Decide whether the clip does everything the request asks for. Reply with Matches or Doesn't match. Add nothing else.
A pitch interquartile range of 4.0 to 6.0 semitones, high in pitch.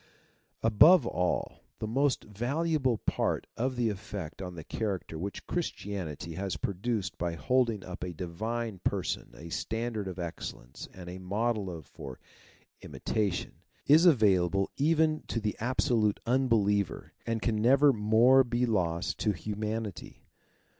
Doesn't match